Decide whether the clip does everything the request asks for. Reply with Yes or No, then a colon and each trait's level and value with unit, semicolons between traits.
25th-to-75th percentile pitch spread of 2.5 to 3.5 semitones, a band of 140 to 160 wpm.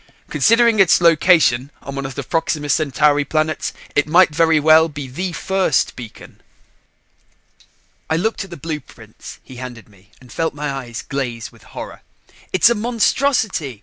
No: average, 4.7 semitones; average, 155 wpm